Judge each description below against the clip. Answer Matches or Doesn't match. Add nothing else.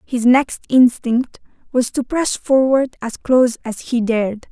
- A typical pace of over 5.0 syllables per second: Doesn't match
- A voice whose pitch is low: Doesn't match